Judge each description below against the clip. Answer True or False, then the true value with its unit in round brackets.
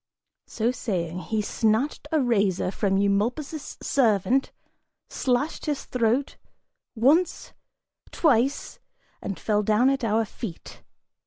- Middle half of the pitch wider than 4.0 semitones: True (4.6 semitones)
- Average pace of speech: False (105 wpm)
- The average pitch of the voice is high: True (230 Hz)